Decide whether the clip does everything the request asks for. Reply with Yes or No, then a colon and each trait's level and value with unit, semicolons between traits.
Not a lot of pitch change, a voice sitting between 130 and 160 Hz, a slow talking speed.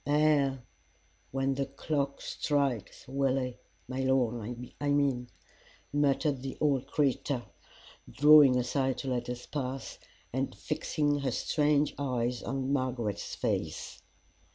Yes: narrow, 2.1 semitones; low, 135 Hz; slow, 115 wpm